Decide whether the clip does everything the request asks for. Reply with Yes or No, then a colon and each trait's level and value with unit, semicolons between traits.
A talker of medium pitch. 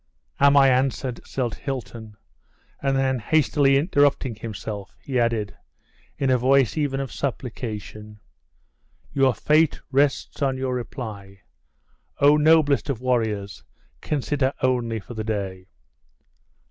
No: low, 130 Hz